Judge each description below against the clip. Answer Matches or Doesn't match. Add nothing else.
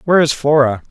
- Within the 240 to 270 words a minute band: Doesn't match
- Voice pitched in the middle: Matches